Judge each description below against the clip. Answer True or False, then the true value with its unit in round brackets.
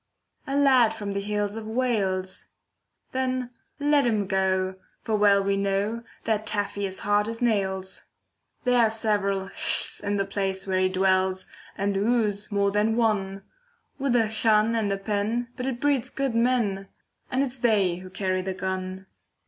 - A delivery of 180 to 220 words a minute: False (170 wpm)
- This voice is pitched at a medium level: False (205 Hz)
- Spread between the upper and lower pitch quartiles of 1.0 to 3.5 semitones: True (3.2 semitones)